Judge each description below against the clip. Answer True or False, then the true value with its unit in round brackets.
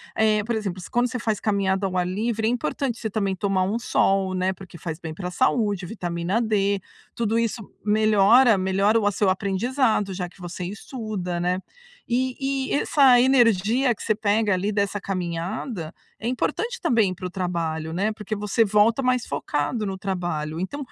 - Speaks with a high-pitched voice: True (205 Hz)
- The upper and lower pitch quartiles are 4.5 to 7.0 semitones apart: False (3.7 semitones)